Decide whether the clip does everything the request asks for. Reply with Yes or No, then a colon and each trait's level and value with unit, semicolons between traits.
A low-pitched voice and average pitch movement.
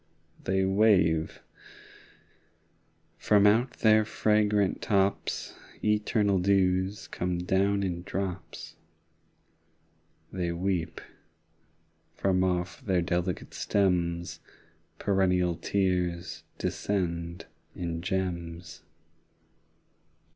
No: very low, 95 Hz; narrow, 2.3 semitones